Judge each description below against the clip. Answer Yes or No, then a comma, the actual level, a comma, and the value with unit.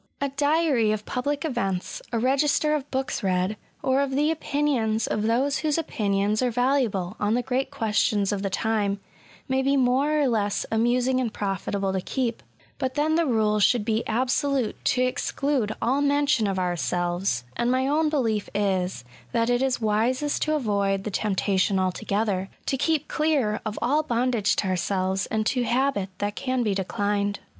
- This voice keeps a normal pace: Yes, average, 175 wpm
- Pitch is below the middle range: No, high, 235 Hz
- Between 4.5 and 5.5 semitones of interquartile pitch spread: Yes, average, 5.1 semitones